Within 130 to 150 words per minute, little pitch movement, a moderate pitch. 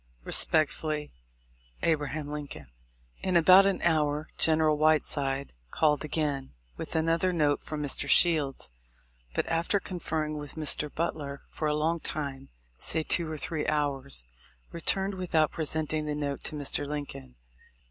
Yes: slow, 135 wpm; narrow, 1.8 semitones; medium, 155 Hz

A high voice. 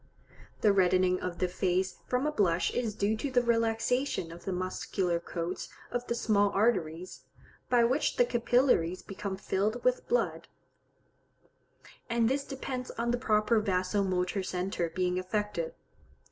Yes: high, 205 Hz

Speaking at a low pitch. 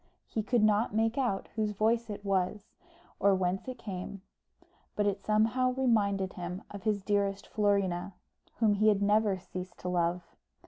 No: high, 205 Hz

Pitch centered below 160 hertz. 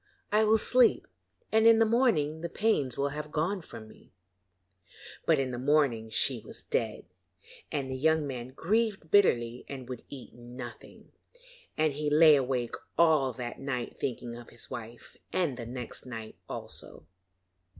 Yes: medium, 140 Hz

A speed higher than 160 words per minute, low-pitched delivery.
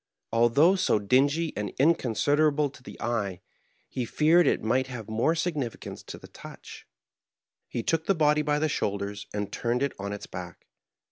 Yes: average, 175 wpm; low, 130 Hz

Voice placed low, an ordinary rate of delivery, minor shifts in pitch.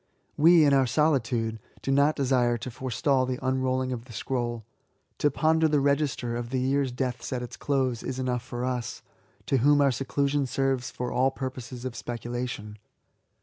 Yes: low, 130 Hz; average, 175 wpm; narrow, 2.1 semitones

